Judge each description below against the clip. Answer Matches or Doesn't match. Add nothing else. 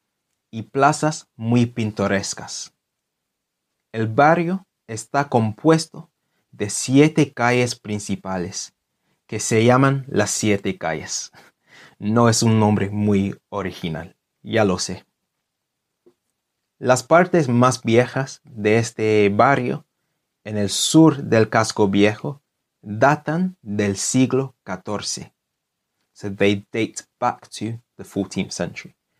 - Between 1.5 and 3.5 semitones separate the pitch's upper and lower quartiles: Doesn't match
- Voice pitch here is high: Doesn't match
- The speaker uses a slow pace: Matches